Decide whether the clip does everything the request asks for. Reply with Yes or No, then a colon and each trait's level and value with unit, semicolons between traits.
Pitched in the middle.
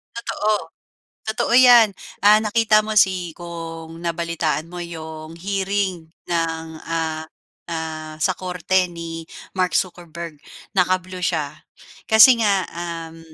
Yes: medium, 175 Hz